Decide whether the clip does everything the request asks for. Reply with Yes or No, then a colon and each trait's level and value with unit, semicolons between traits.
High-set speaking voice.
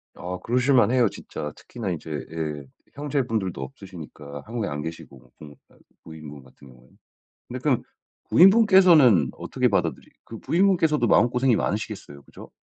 No: very low, 95 Hz